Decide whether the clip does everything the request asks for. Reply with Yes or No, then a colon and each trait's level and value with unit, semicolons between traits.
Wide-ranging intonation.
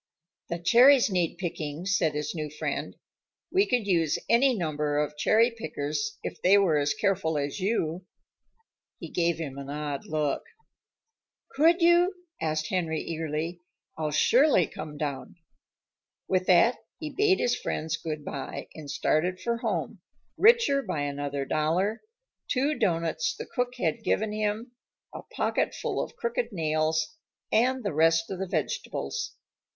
Yes: wide, 7.1 semitones